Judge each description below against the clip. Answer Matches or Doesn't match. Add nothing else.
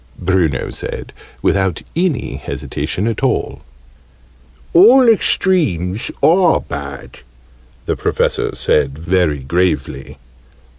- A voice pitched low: Matches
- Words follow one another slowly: Matches